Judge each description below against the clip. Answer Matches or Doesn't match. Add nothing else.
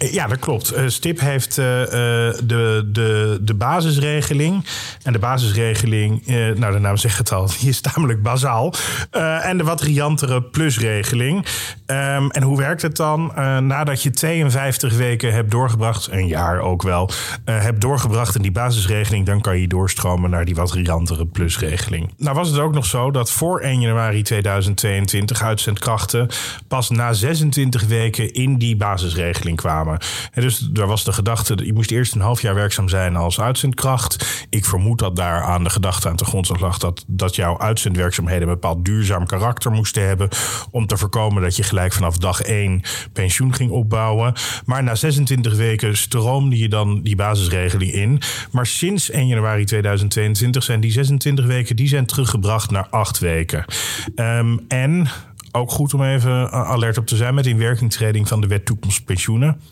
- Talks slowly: Doesn't match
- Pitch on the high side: Doesn't match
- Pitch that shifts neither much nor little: Matches